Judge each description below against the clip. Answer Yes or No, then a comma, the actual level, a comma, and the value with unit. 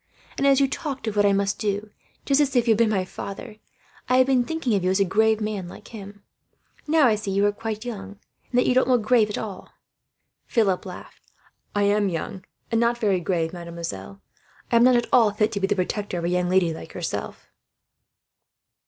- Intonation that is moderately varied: Yes, average, 3.7 semitones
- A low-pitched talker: No, high, 210 Hz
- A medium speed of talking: No, fast, 225 wpm